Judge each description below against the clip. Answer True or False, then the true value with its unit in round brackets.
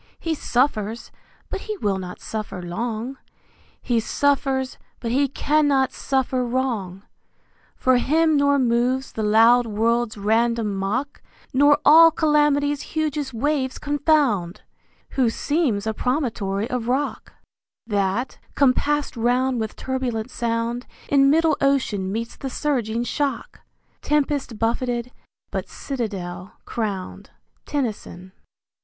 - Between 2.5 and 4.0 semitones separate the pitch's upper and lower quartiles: False (4.4 semitones)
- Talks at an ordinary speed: False (115 wpm)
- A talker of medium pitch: False (250 Hz)